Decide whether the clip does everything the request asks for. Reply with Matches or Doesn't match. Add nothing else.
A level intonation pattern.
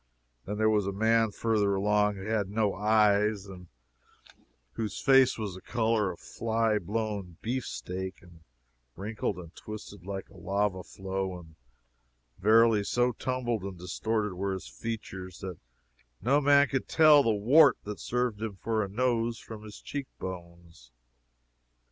Doesn't match